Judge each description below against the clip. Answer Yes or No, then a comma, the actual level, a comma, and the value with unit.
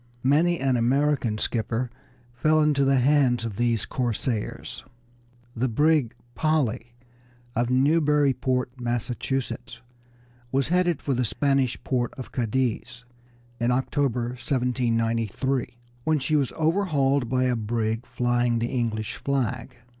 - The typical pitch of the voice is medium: No, low, 125 Hz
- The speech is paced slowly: Yes, slow, 115 wpm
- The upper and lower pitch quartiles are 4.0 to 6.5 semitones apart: No, average, 2.7 semitones